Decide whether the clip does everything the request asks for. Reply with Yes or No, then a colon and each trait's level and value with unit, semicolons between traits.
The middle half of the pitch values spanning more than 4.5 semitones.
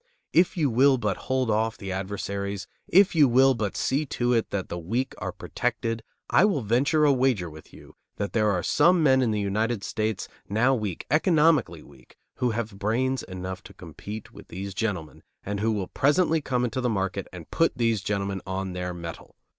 Yes: average, 5.1 semitones